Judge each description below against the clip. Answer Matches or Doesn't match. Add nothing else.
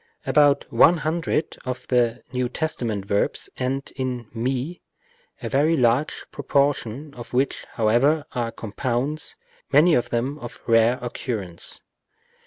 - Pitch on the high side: Doesn't match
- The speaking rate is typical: Doesn't match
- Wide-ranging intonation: Doesn't match